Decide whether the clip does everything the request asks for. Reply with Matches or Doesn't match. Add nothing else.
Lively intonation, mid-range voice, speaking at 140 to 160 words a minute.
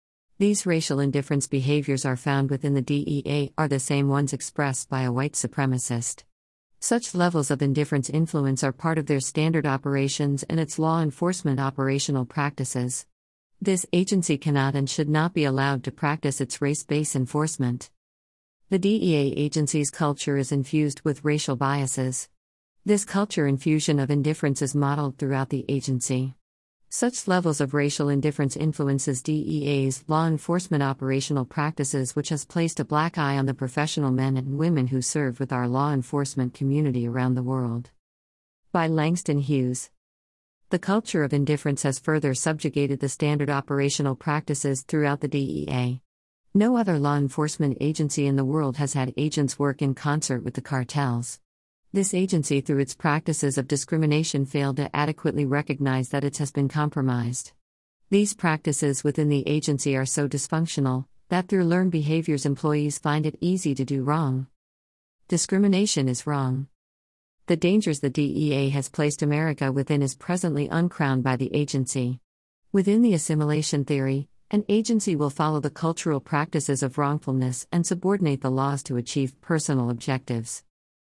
Doesn't match